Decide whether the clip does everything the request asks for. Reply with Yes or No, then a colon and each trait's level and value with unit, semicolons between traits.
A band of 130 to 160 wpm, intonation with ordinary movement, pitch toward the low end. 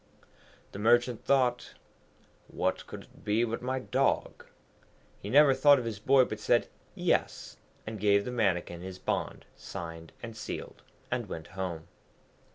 Yes: average, 150 wpm; average, 4.6 semitones; low, 110 Hz